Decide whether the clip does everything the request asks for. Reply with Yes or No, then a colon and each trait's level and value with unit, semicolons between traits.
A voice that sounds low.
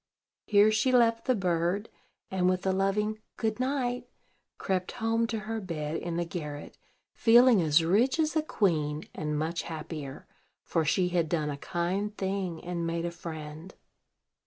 No: medium, 185 Hz